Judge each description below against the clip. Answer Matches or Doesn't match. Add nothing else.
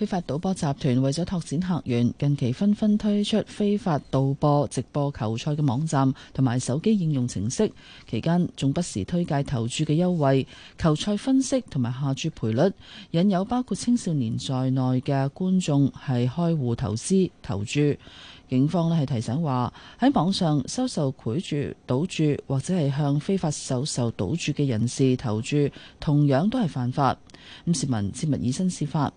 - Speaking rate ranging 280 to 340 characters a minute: Doesn't match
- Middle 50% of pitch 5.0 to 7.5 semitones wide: Matches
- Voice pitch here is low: Doesn't match